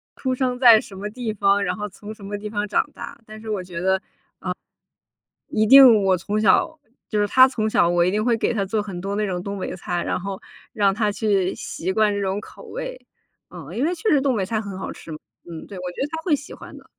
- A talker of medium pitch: No, high, 210 Hz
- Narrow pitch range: No, average, 3.2 semitones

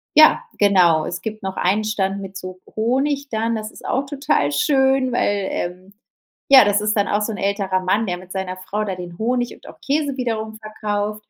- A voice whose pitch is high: Yes, high, 210 Hz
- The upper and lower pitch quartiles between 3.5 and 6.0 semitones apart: Yes, average, 4.1 semitones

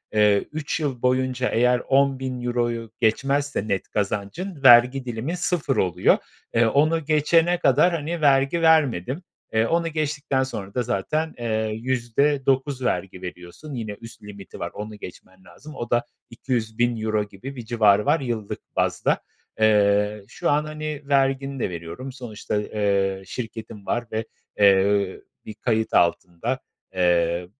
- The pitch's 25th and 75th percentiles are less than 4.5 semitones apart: No, average, 5.1 semitones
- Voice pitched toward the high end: No, low, 120 Hz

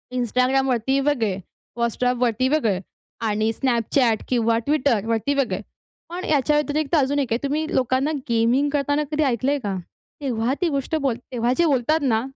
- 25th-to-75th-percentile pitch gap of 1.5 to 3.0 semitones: No, average, 3.7 semitones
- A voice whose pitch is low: No, very high, 260 Hz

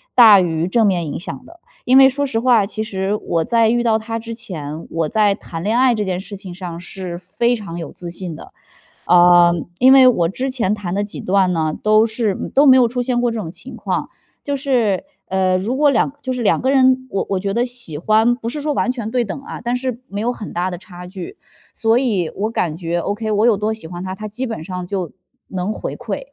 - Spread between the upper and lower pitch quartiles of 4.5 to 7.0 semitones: Yes, average, 5.0 semitones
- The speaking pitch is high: Yes, high, 210 Hz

